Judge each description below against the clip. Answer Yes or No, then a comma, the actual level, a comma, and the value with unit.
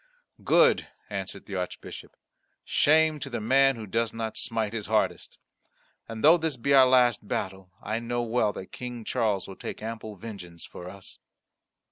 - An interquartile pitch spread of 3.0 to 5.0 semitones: Yes, average, 3.4 semitones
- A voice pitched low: Yes, low, 115 Hz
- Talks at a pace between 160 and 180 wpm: Yes, average, 165 wpm